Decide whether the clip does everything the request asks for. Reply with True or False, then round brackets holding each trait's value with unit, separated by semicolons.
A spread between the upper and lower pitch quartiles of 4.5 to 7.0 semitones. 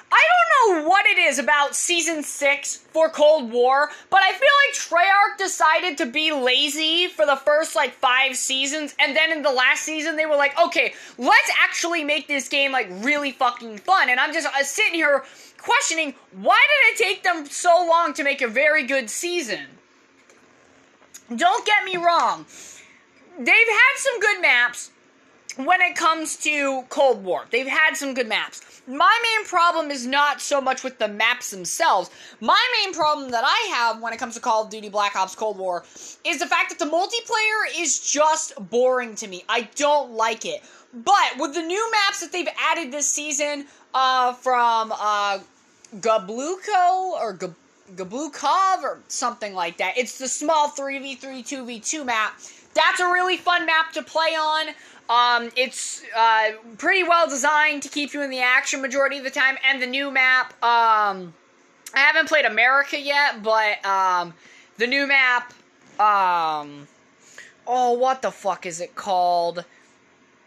True (5.2 semitones)